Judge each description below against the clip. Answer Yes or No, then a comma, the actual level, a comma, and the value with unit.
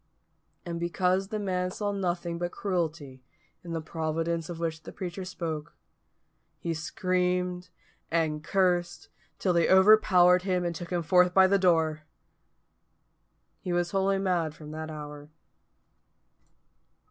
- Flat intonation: Yes, narrow, 2.2 semitones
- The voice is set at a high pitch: No, medium, 175 Hz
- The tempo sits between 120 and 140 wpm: Yes, slow, 135 wpm